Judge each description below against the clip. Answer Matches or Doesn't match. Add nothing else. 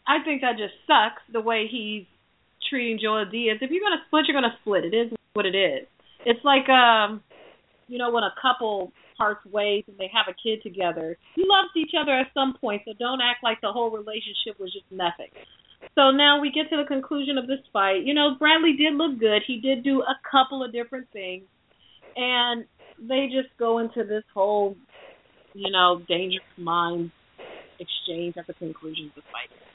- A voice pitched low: Doesn't match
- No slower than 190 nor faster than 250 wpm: Matches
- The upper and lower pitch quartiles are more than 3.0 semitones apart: Matches